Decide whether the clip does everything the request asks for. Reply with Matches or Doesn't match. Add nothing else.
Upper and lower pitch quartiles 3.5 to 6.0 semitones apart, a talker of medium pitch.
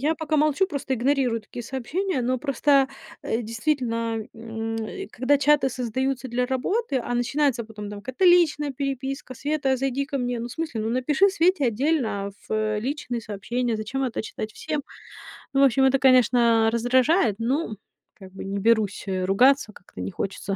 Doesn't match